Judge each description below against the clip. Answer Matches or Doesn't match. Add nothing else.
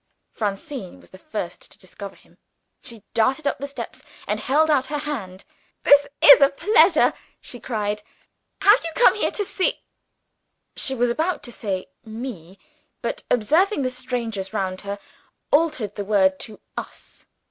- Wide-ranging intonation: Matches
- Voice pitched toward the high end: Matches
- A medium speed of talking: Matches